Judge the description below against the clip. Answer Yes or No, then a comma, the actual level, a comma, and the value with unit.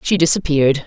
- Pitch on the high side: No, medium, 155 Hz